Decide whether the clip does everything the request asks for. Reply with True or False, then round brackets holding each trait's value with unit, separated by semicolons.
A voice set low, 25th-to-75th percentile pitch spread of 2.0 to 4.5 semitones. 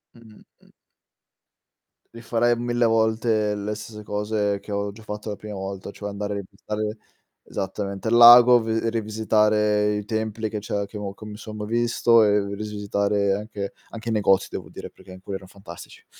False (105 Hz; 1.6 semitones)